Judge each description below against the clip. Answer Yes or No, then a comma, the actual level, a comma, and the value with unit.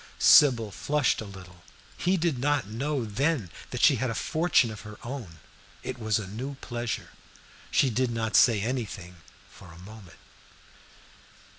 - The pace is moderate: Yes, average, 155 wpm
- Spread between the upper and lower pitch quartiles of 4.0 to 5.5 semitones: Yes, average, 4.7 semitones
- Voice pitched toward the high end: No, low, 115 Hz